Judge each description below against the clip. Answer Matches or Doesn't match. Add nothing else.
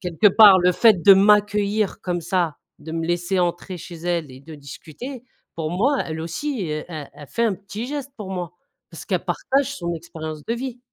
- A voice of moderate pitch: Matches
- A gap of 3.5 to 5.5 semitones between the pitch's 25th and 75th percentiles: Matches